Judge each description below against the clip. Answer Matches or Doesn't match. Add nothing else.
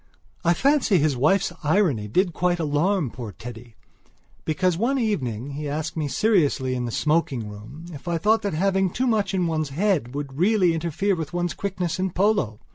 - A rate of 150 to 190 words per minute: Matches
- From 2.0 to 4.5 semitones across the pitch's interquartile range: Doesn't match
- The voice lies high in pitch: Doesn't match